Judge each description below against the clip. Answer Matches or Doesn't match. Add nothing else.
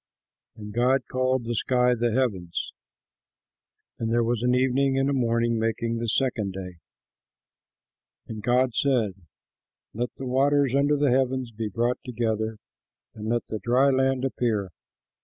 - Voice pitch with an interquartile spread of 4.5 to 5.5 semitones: Doesn't match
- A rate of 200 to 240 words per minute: Doesn't match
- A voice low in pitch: Matches